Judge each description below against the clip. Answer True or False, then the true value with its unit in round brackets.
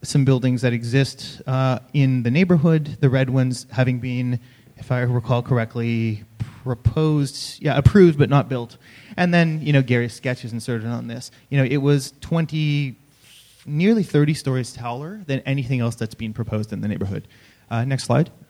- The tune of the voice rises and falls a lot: False (3.2 semitones)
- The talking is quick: False (170 wpm)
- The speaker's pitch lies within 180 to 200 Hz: False (130 Hz)